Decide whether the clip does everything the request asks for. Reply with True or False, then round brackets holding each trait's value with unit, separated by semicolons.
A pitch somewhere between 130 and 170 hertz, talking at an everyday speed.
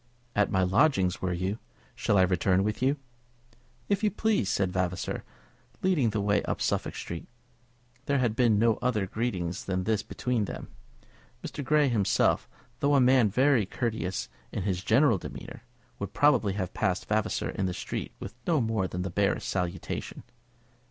False (105 Hz; 165 wpm)